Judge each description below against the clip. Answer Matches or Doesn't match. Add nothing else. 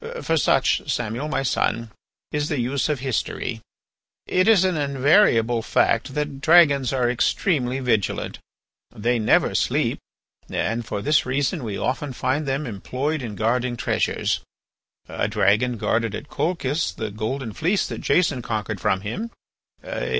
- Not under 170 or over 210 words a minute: Doesn't match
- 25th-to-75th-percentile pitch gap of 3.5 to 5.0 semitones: Matches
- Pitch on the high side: Doesn't match